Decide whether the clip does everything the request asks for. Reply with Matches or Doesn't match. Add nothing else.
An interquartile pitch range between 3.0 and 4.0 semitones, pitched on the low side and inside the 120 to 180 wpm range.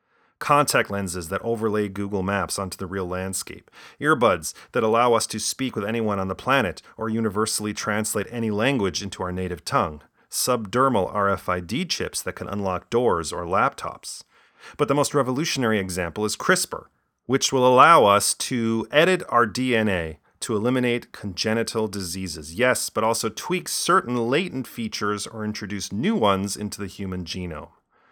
Matches